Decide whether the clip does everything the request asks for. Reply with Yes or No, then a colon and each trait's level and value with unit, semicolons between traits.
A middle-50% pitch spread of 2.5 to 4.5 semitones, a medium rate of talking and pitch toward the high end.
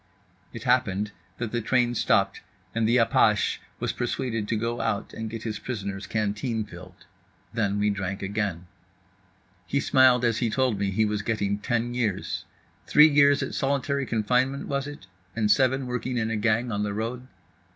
No: average, 3.2 semitones; average, 170 wpm; low, 115 Hz